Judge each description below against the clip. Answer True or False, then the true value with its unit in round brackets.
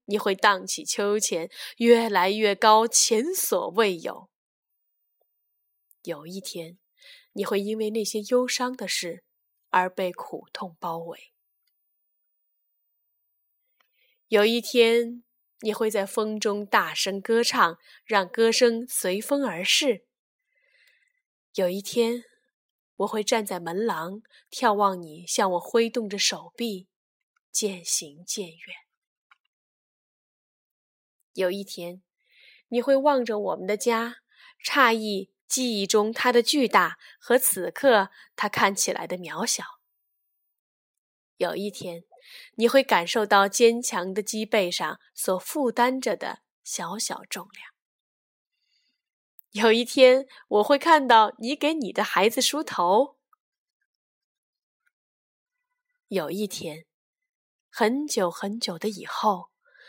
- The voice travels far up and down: False (4.7 semitones)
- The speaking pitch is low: False (220 Hz)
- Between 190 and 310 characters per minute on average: False (155 characters per minute)